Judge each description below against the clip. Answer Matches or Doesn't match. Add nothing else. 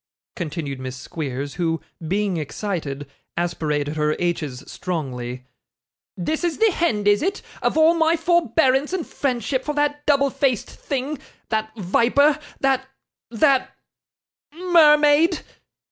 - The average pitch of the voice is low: Doesn't match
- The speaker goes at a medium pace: Doesn't match